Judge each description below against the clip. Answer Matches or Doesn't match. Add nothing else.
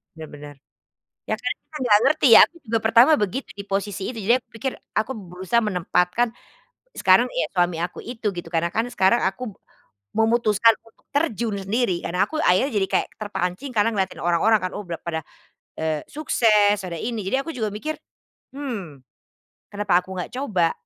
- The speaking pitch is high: Matches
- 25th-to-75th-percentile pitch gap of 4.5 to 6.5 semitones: Matches